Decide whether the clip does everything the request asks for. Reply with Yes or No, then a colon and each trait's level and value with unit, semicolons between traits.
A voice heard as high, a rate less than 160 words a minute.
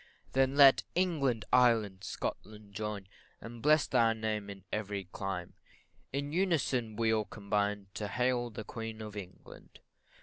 No: low, 110 Hz; average, 140 wpm